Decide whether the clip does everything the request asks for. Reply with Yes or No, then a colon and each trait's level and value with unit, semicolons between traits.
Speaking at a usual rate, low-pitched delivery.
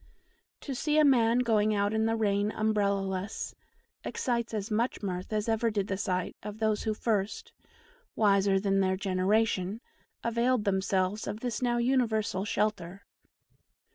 No: average, 150 wpm; high, 210 Hz